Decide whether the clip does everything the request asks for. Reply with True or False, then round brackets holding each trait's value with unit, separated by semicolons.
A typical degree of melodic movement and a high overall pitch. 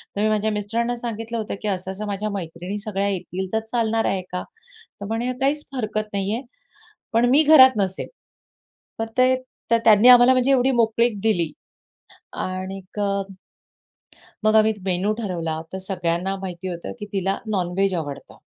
True (3.5 semitones; 210 Hz)